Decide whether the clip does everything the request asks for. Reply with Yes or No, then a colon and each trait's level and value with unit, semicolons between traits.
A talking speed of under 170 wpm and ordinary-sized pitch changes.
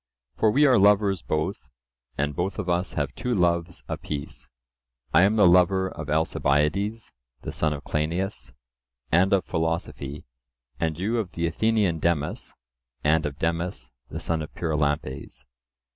Yes: average, 145 wpm; average, 4.4 semitones